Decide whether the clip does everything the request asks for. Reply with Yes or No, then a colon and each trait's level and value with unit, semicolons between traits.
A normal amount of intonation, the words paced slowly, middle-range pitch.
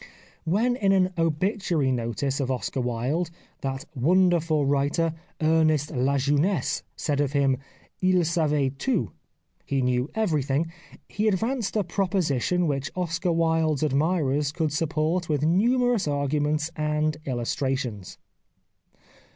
Yes: average, 4.4 semitones; slow, 120 wpm; medium, 155 Hz